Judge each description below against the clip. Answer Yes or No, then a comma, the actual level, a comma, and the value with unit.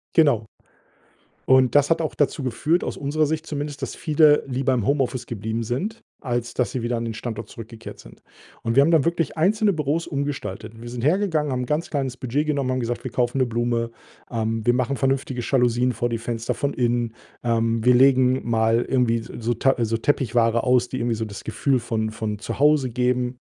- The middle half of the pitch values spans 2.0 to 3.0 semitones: No, average, 3.5 semitones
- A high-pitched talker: No, low, 125 Hz